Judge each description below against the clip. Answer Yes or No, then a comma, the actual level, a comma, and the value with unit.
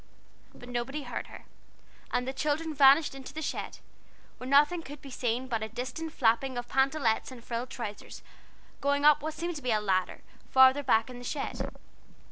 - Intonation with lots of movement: No, average, 3.2 semitones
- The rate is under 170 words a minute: No, average, 185 wpm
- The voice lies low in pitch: No, very high, 265 Hz